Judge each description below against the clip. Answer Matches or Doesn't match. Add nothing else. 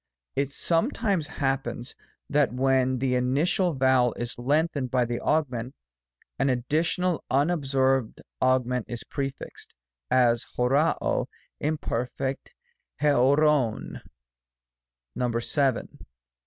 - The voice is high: Doesn't match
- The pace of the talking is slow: Matches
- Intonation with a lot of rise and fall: Doesn't match